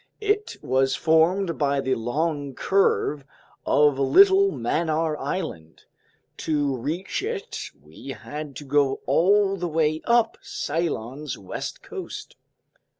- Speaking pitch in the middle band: Yes, medium, 155 Hz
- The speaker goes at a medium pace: No, slow, 115 wpm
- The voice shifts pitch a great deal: No, average, 4.7 semitones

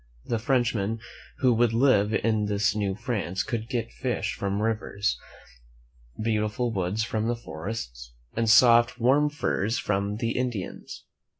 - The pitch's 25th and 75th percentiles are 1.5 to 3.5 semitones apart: Yes, average, 2.7 semitones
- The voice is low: Yes, low, 110 Hz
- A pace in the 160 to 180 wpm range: No, average, 140 wpm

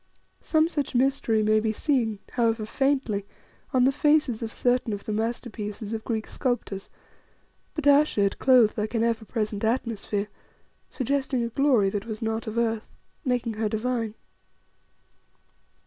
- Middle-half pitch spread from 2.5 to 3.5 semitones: Yes, average, 3.0 semitones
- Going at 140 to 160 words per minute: Yes, average, 150 wpm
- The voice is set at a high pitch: Yes, high, 230 Hz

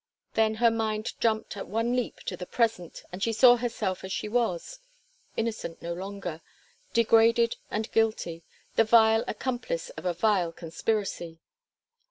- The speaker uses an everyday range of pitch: Yes, average, 3.8 semitones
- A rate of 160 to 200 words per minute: No, average, 150 wpm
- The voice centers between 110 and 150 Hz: No, high, 220 Hz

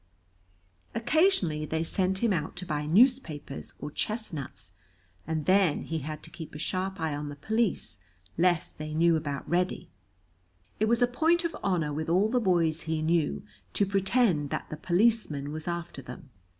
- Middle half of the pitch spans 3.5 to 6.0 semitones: Yes, average, 4.7 semitones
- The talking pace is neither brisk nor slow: Yes, average, 170 wpm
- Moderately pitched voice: Yes, medium, 170 Hz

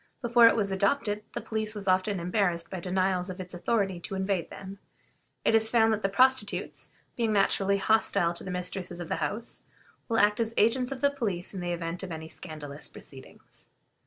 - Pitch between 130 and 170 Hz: No, high, 195 Hz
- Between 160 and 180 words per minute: No, average, 195 wpm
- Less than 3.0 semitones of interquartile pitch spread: No, average, 3.6 semitones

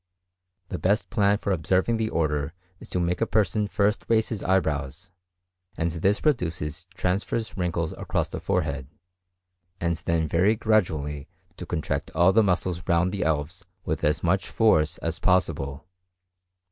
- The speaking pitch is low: Yes, very low, 90 Hz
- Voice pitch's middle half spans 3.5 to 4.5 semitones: Yes, average, 4.1 semitones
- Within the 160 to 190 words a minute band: No, average, 150 wpm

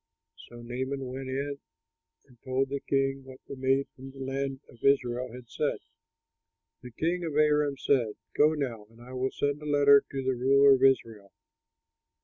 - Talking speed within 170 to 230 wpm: Yes, average, 175 wpm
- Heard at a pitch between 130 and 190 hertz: Yes, low, 135 Hz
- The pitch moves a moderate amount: No, narrow, 1.8 semitones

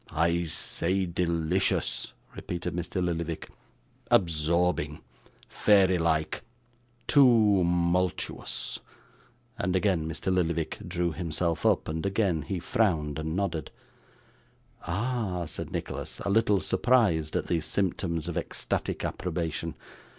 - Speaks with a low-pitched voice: Yes, very low, 85 Hz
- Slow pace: Yes, slow, 105 wpm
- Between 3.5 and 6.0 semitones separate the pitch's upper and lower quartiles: No, average, 2.7 semitones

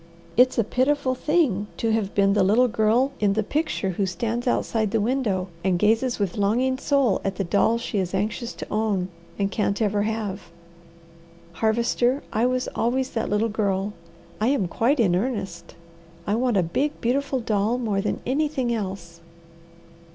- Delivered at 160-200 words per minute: Yes, average, 170 wpm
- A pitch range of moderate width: Yes, average, 3.9 semitones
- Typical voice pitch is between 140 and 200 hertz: No, high, 220 Hz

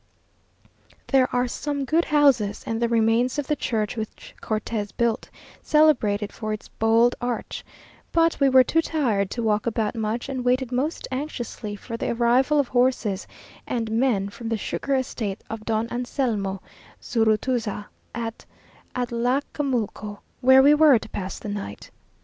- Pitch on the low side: No, high, 235 Hz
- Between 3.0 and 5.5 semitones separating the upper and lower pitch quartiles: Yes, average, 3.3 semitones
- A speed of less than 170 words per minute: Yes, average, 150 wpm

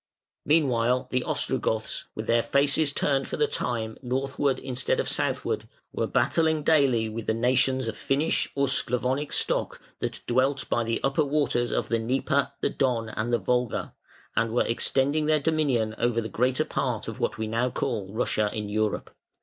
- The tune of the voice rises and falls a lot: No, average, 3.3 semitones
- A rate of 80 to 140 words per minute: No, average, 175 wpm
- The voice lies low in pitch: Yes, low, 125 Hz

